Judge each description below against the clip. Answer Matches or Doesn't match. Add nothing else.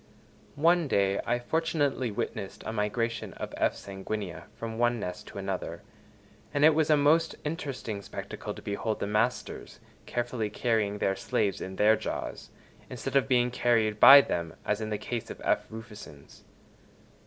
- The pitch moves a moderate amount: Matches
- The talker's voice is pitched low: Matches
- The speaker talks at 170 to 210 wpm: Doesn't match